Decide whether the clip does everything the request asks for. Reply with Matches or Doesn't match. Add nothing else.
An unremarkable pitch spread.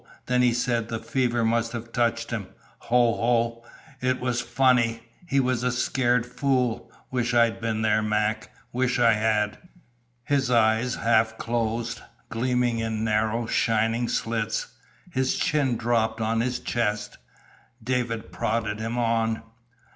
Doesn't match